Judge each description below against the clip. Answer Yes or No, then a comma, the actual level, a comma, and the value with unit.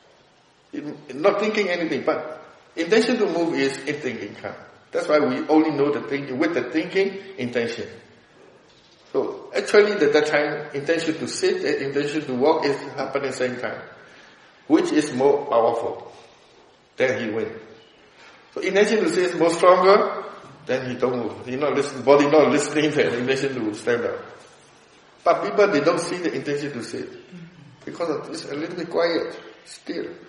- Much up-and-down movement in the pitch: Yes, wide, 6.3 semitones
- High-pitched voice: No, medium, 155 Hz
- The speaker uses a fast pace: No, average, 175 wpm